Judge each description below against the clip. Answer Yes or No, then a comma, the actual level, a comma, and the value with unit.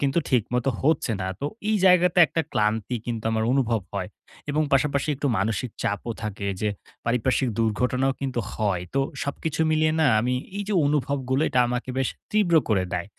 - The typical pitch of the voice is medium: No, low, 125 Hz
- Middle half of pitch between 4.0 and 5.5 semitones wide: Yes, average, 4.6 semitones